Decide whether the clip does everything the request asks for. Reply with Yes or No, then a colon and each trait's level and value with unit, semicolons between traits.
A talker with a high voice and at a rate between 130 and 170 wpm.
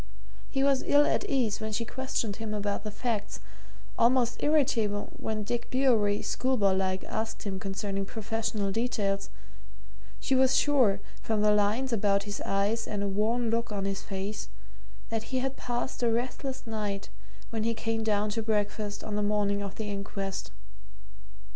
Yes: high, 215 Hz; average, 165 wpm